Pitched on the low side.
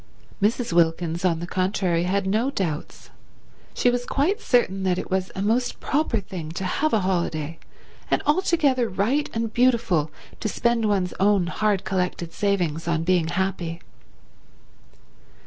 No: high, 190 Hz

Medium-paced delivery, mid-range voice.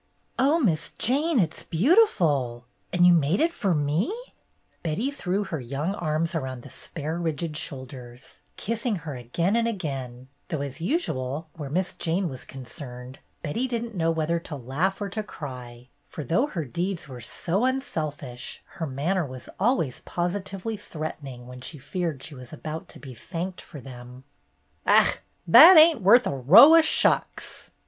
Yes: average, 170 wpm; medium, 160 Hz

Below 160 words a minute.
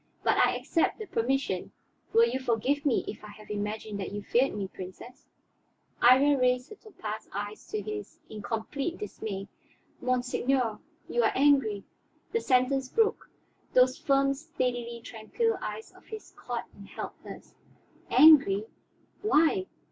Yes: average, 150 wpm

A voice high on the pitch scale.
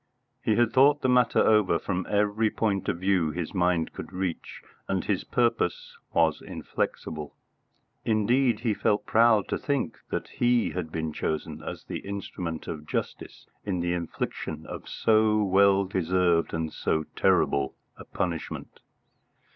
No: very low, 95 Hz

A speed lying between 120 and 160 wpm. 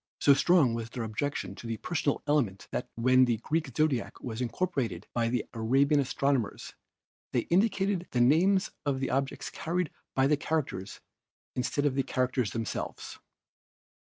Yes: average, 155 wpm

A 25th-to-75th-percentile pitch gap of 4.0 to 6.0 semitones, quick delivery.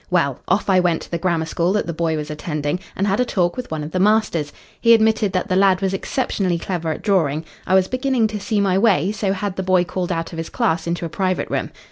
No: average, 3.3 semitones; fast, 260 wpm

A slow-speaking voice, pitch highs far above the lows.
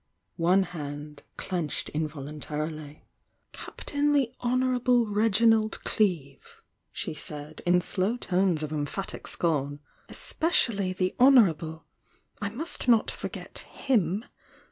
Yes: slow, 100 wpm; wide, 7.0 semitones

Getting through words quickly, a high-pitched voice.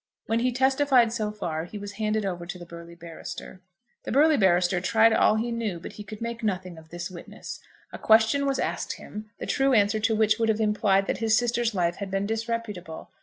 Yes: fast, 220 wpm; high, 215 Hz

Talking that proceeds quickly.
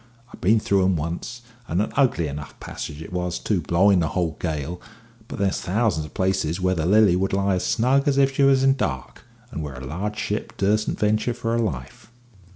Yes: fast, 215 wpm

